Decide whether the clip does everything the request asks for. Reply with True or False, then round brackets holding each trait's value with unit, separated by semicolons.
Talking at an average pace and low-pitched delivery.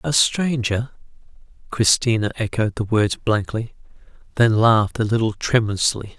False (115 wpm; 115 Hz)